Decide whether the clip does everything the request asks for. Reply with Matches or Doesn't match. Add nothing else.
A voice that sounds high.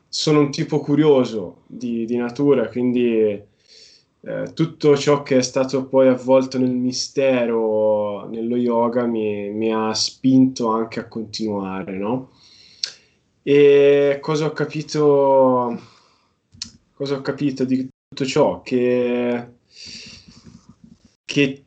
Doesn't match